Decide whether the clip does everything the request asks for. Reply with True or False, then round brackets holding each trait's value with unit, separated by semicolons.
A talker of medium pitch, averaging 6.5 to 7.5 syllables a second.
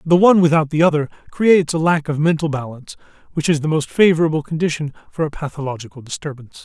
True (155 Hz; 6.9 syllables/s)